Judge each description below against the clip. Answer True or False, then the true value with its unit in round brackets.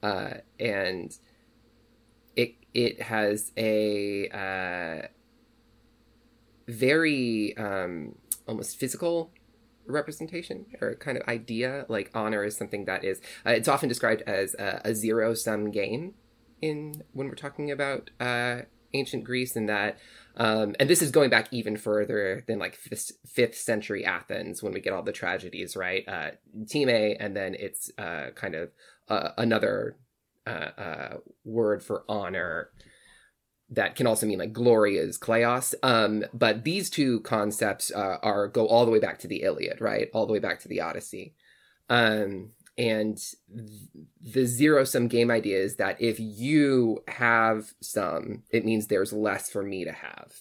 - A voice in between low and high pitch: False (115 Hz)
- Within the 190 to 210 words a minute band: False (155 wpm)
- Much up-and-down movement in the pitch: False (3.2 semitones)